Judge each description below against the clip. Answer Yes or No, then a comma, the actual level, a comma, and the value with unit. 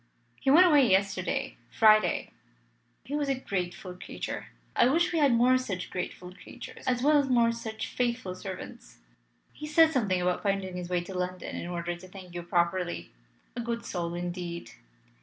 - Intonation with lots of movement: Yes, wide, 5.9 semitones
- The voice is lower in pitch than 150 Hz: No, high, 195 Hz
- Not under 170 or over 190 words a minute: Yes, average, 175 wpm